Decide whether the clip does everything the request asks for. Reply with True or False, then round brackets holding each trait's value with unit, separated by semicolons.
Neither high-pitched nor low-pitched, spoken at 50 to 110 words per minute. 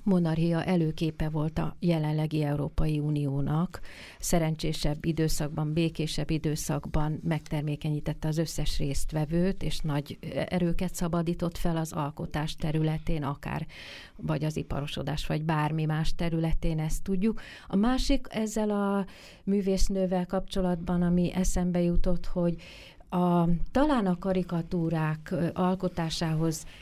True (165 Hz; 105 wpm)